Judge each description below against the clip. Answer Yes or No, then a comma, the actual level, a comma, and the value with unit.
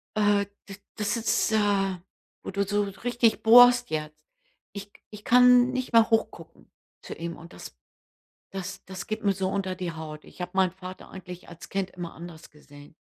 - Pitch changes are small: No, average, 3.4 semitones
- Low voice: No, high, 195 Hz